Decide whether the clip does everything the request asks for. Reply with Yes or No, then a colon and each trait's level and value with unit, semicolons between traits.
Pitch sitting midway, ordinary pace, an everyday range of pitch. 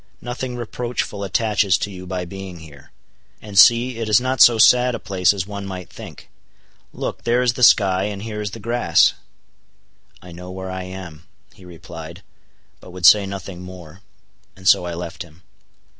No: very low, 95 Hz; average, 180 wpm; average, 3.8 semitones